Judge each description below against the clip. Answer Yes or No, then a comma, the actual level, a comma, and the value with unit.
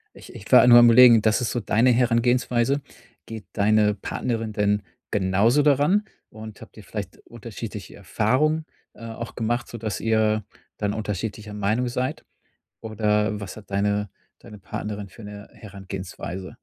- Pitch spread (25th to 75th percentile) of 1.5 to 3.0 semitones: Yes, narrow, 2.4 semitones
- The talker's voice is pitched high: No, low, 110 Hz